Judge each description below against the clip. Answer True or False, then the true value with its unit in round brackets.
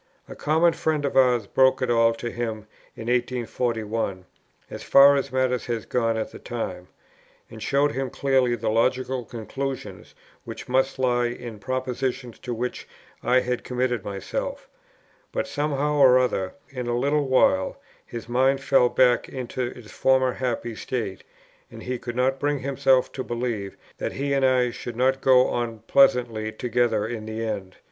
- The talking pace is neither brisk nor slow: True (165 wpm)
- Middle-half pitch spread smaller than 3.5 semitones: True (2.4 semitones)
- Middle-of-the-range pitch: False (125 Hz)